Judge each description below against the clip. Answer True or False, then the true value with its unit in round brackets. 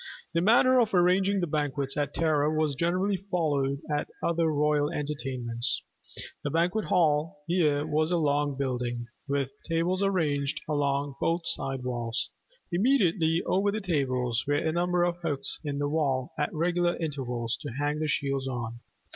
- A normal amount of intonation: True (3.9 semitones)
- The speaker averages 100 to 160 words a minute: True (155 wpm)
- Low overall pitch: False (150 Hz)